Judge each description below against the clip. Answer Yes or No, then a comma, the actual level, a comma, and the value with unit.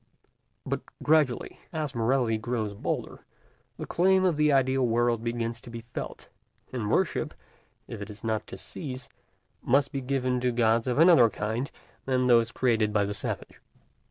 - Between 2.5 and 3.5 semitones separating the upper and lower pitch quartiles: Yes, average, 2.9 semitones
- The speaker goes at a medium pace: Yes, average, 160 wpm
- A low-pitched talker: Yes, low, 120 Hz